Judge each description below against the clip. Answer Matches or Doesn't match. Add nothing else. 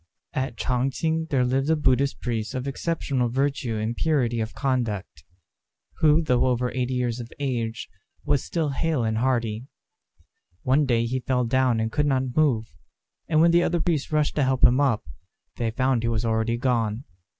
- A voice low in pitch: Matches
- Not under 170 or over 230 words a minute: Matches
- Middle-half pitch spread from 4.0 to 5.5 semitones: Doesn't match